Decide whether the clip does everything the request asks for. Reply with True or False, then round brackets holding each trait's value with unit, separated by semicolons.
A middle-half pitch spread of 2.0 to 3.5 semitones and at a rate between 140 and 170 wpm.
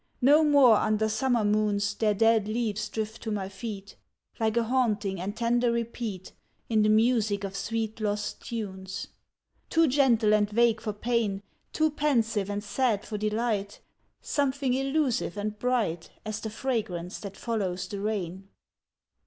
True (2.6 semitones; 150 wpm)